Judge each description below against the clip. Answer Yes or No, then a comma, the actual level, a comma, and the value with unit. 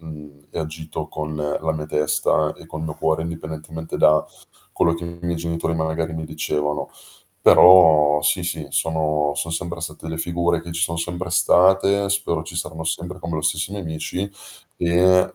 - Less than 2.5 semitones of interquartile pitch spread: Yes, narrow, 1.8 semitones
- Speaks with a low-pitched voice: Yes, very low, 80 Hz